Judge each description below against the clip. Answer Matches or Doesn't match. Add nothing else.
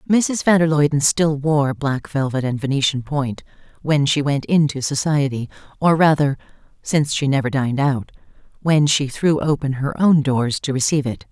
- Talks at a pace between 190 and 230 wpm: Doesn't match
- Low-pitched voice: Doesn't match